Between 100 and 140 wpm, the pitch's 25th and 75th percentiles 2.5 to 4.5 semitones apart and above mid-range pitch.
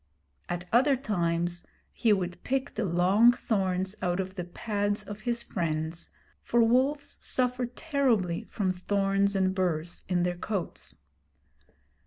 No: slow, 135 wpm; average, 5.0 semitones; high, 195 Hz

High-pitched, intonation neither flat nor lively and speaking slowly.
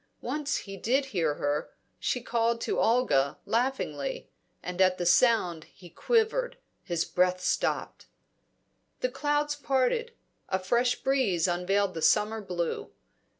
No: high, 225 Hz; wide, 7.0 semitones; slow, 130 wpm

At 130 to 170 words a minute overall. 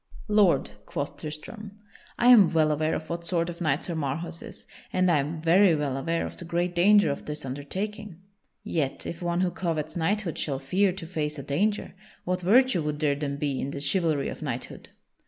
No: average, 200 wpm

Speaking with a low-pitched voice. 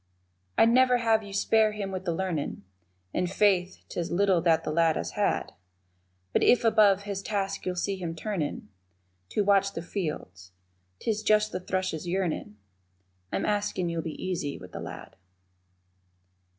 No: high, 190 Hz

